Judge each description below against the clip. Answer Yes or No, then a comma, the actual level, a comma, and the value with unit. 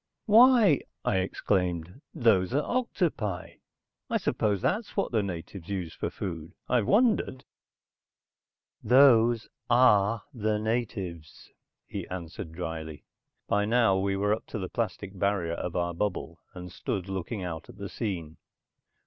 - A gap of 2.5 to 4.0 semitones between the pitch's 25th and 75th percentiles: No, average, 4.9 semitones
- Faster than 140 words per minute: No, slow, 135 wpm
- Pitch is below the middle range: Yes, low, 100 Hz